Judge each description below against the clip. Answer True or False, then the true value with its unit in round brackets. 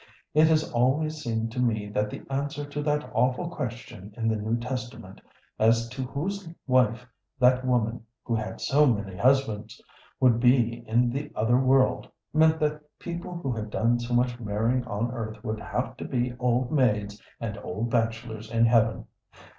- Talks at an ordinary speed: True (170 wpm)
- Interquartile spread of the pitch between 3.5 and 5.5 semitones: False (3.0 semitones)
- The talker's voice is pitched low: True (120 Hz)